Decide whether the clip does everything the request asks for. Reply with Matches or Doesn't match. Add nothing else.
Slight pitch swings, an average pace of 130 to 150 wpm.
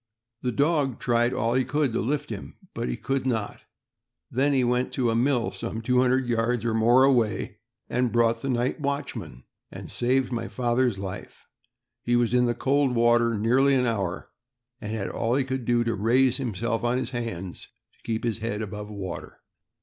Doesn't match